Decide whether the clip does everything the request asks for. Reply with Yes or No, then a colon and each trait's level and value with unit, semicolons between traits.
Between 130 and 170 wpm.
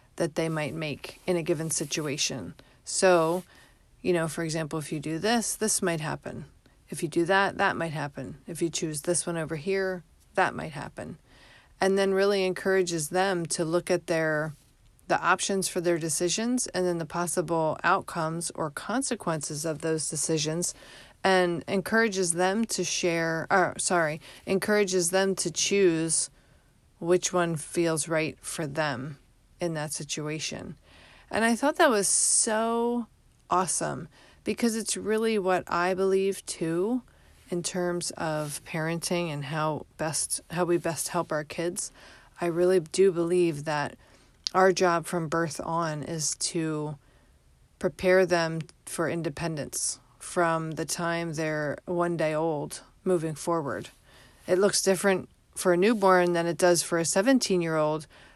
Yes: average, 150 wpm